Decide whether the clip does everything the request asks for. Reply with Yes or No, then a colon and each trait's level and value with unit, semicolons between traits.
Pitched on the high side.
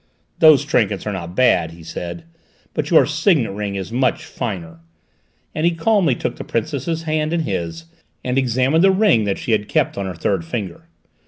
No: low, 125 Hz